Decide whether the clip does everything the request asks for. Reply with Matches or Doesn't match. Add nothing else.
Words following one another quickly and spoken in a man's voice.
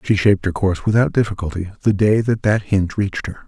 Matches